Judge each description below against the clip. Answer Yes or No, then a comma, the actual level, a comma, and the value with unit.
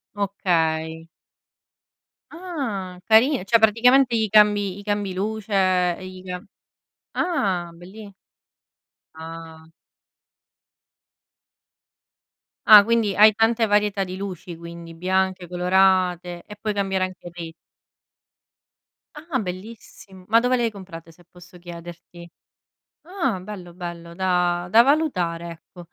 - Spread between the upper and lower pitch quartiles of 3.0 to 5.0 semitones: Yes, average, 3.5 semitones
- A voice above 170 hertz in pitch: Yes, high, 190 Hz